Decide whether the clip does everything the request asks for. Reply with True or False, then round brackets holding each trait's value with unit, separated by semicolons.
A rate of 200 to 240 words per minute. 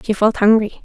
True (215 wpm)